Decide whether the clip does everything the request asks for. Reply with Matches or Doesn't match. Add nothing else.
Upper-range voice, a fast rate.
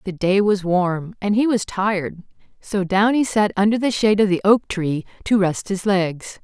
Matches